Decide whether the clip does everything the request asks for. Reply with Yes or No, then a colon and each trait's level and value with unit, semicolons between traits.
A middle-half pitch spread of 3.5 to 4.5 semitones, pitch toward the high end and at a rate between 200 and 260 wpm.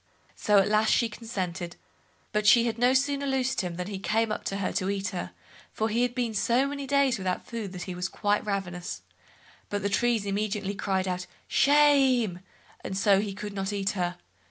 Yes: average, 3.8 semitones; high, 210 Hz; fast, 205 wpm